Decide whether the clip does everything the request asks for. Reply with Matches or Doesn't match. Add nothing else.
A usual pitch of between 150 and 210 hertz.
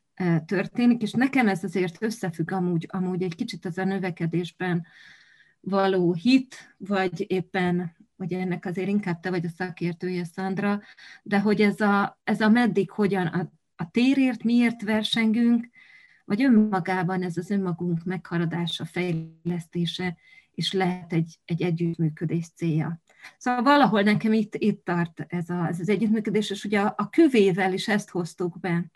Matches